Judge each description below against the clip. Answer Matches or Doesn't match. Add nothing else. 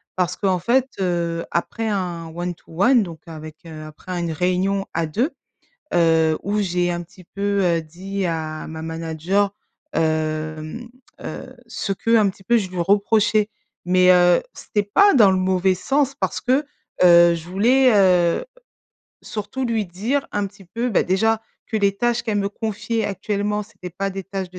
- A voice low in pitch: Doesn't match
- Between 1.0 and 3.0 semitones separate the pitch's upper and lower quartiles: Doesn't match